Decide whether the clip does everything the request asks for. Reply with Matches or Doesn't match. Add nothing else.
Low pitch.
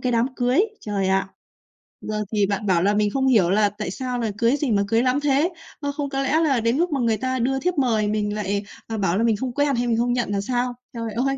Doesn't match